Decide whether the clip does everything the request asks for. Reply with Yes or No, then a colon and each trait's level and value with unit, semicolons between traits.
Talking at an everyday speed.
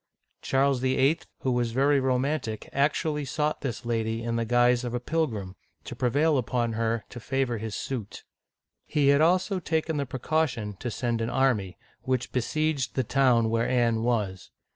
Yes: average, 165 wpm